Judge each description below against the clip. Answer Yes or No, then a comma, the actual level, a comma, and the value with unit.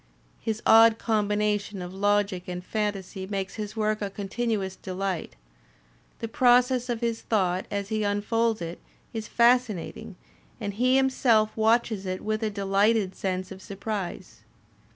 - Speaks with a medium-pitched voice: No, high, 210 Hz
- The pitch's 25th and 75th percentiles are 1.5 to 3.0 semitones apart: Yes, narrow, 2.6 semitones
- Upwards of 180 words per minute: No, average, 140 wpm